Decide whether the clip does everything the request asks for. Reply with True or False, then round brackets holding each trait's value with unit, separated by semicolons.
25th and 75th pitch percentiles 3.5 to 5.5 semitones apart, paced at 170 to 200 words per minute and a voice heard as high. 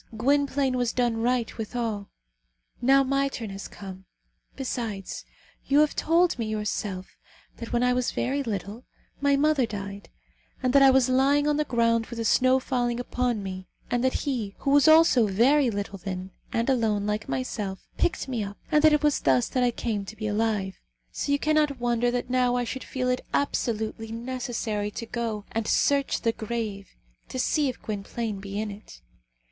True (3.9 semitones; 185 wpm; 235 Hz)